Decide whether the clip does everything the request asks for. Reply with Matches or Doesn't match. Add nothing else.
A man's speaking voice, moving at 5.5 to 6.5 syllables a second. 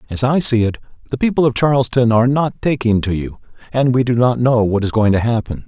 Matches